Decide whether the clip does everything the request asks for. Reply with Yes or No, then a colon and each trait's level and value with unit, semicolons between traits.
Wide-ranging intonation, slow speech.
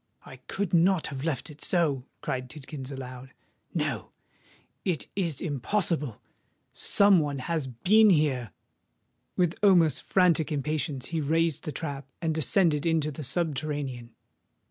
No: average, 4.0 semitones; slow, 125 wpm